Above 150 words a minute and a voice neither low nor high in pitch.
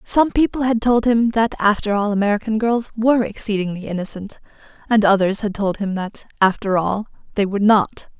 No: average, 175 wpm; high, 210 Hz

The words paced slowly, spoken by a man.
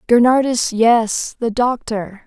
No: slow, 105 wpm; female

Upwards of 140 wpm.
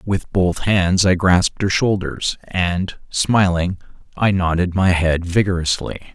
No: slow, 135 wpm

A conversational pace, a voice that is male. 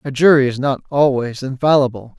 Yes: average, 165 wpm; male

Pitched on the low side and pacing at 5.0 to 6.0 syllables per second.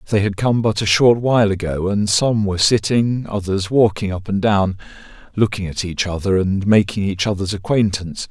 Yes: low, 100 Hz; 5.2 syllables/s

